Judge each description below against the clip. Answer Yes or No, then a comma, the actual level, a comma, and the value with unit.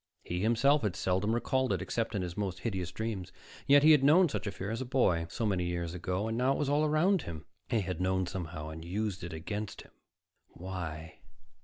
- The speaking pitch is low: Yes, low, 100 Hz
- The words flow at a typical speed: No, fast, 215 wpm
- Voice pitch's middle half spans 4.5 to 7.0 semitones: Yes, wide, 5.6 semitones